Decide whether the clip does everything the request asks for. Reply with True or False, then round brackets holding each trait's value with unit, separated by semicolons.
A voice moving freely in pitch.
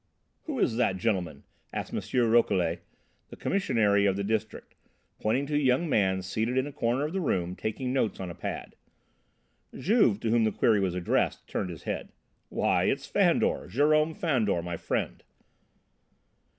True (6.4 semitones)